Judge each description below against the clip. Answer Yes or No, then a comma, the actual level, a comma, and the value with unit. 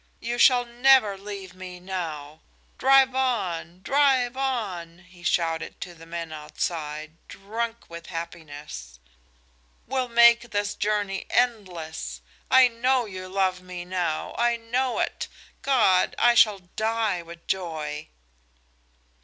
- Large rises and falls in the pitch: Yes, wide, 5.9 semitones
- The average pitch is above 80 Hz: Yes, high, 190 Hz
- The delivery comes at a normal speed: No, slow, 120 wpm